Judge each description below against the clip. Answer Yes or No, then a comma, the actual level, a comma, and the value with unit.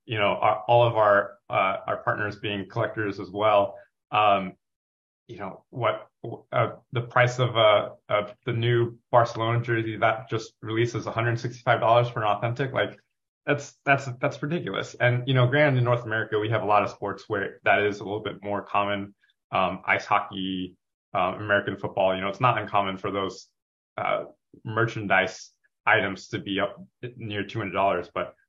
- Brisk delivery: No, average, 175 wpm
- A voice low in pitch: Yes, low, 110 Hz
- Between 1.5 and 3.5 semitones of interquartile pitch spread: Yes, average, 2.9 semitones